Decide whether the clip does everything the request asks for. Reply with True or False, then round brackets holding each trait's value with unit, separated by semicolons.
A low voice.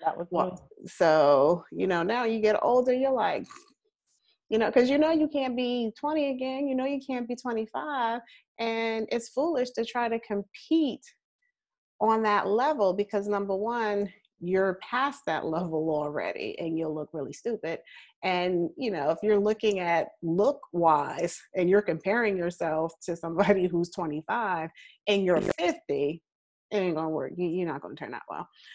False (205 Hz)